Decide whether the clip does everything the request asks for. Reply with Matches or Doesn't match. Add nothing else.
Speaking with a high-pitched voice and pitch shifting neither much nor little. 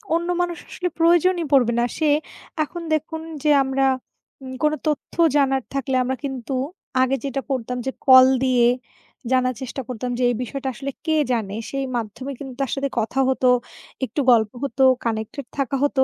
Doesn't match